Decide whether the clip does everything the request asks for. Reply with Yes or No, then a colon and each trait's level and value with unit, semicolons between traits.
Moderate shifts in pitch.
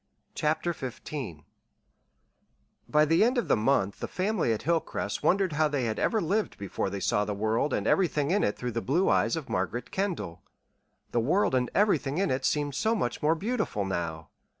No: wide, 8.5 semitones